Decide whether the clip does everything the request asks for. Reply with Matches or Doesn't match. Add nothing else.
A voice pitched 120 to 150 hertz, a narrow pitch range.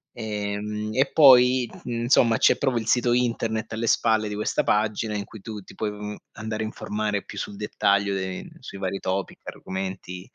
Doesn't match